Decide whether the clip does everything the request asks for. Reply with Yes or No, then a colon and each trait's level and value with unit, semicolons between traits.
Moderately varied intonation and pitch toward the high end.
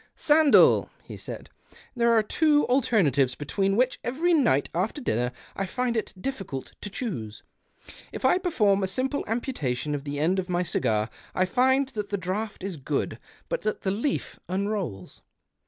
No: wide, 8.3 semitones; high, 200 Hz